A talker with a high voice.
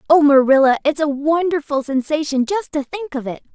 Yes: very high, 295 Hz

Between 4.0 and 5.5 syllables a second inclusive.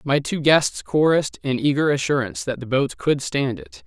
Yes: 5.1 syllables/s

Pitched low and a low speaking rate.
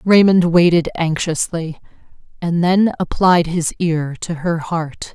No: medium, 170 Hz; slow, 130 wpm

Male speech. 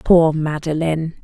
No: female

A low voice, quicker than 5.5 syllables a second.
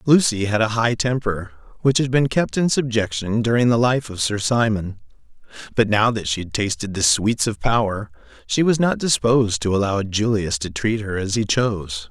No: low, 110 Hz; 4.9 syllables/s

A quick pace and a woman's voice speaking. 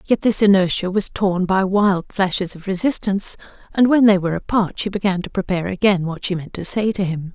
Yes: fast, 220 wpm; female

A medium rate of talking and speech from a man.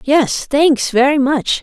No: average, 150 wpm; female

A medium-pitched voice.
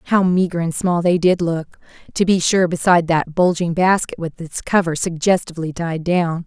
Yes: medium, 170 Hz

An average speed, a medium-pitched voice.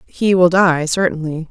Yes: average, 160 wpm; medium, 170 Hz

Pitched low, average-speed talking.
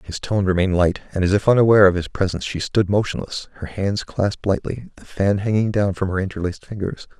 No: very low, 95 Hz; fast, 215 wpm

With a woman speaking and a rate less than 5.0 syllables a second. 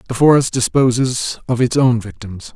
No: male; 4.8 syllables/s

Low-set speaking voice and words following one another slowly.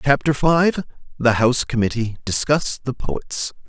Yes: low, 130 Hz; slow, 130 wpm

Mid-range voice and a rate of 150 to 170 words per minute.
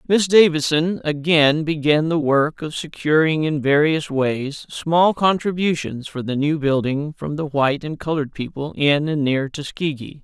Yes: medium, 150 Hz; average, 160 wpm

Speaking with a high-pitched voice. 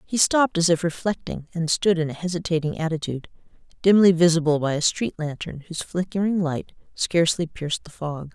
No: medium, 170 Hz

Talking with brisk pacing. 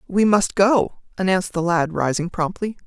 No: average, 165 wpm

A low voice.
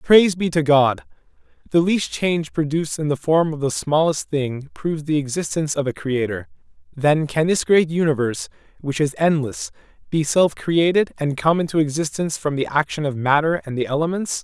No: medium, 150 Hz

